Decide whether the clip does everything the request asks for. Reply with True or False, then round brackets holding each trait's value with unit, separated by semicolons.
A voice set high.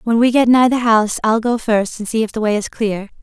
True (225 Hz)